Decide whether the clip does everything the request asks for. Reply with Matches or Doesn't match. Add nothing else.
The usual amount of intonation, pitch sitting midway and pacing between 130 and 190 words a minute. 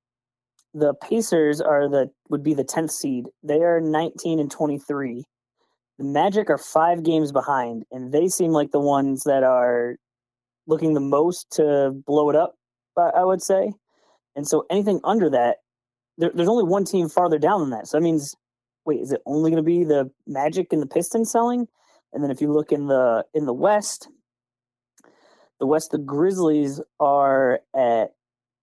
Matches